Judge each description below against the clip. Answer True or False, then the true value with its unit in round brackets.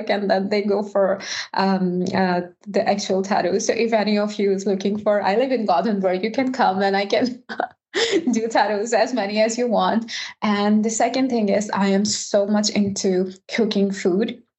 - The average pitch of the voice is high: True (205 Hz)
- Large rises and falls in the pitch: False (2.4 semitones)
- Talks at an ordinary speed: True (195 wpm)